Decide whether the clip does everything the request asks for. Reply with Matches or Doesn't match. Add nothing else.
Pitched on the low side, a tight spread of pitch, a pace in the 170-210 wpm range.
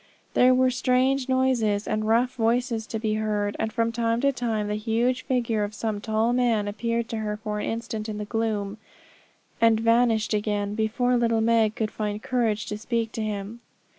Doesn't match